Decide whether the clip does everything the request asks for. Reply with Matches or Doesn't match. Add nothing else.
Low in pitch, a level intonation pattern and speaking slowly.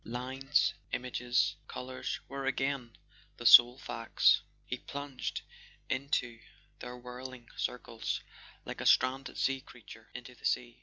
Matches